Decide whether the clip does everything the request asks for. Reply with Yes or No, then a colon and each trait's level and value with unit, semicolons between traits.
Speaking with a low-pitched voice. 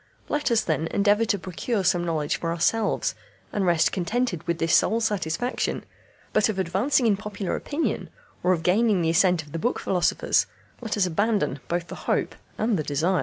No: high, 190 Hz